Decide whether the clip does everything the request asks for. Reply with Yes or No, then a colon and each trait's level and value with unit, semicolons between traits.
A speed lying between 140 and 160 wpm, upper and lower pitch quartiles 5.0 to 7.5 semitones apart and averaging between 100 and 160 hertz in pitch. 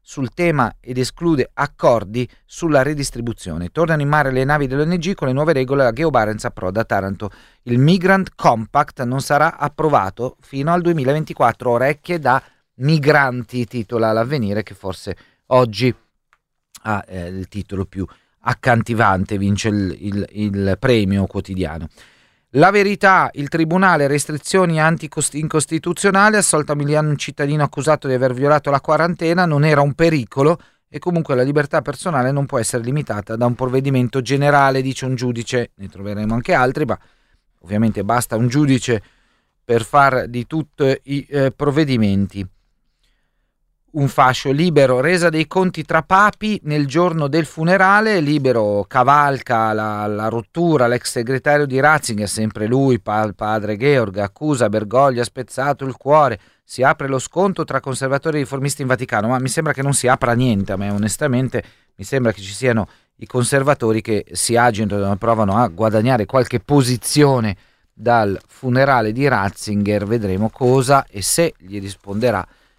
Yes: average, 150 wpm; average, 5.3 semitones; low, 130 Hz